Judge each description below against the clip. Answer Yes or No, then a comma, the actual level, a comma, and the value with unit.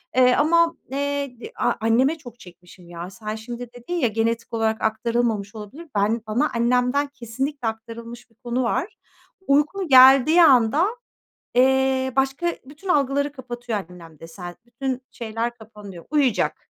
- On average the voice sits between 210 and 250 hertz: Yes, high, 245 Hz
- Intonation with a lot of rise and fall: No, average, 3.8 semitones